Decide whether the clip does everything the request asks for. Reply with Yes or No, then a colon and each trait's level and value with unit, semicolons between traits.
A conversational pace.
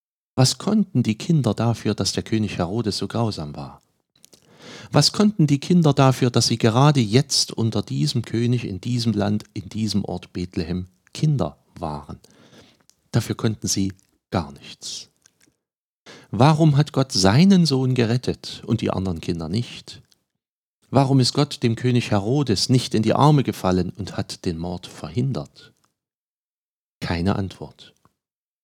Yes: average, 140 wpm